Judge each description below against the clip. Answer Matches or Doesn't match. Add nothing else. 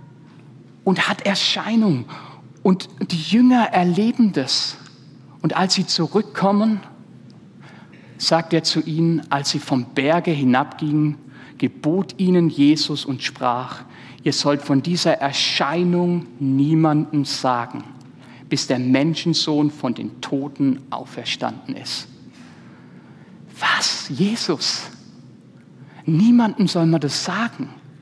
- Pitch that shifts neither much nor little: Matches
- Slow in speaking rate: Matches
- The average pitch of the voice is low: Doesn't match